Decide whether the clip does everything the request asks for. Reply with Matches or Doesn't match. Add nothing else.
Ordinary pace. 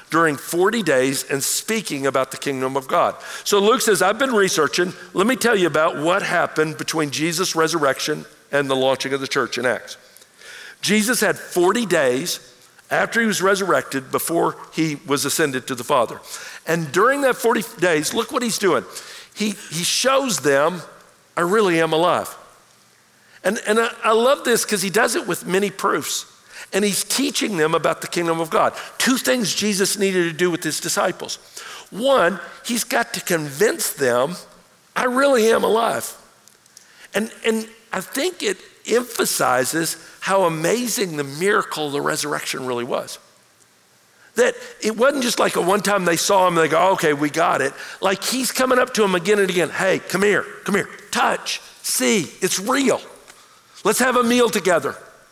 Matches